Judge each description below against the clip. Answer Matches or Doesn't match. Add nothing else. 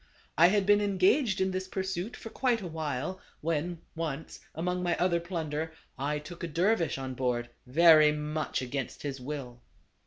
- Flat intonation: Doesn't match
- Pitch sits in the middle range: Matches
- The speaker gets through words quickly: Doesn't match